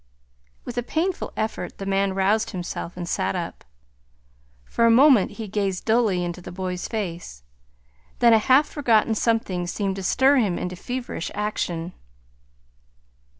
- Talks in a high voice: Yes, high, 200 Hz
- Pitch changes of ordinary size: Yes, average, 4.3 semitones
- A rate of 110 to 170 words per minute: Yes, average, 150 wpm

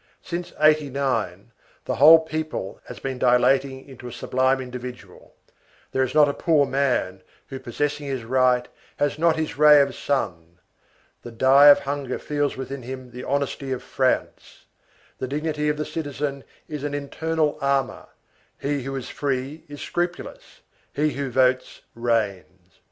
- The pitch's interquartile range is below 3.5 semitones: Yes, narrow, 2.5 semitones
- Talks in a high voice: No, low, 135 Hz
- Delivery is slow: No, average, 150 wpm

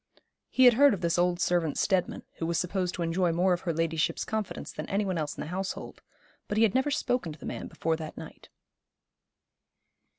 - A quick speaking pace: Yes, fast, 210 wpm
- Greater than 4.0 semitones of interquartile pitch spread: No, average, 3.7 semitones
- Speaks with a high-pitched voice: No, medium, 180 Hz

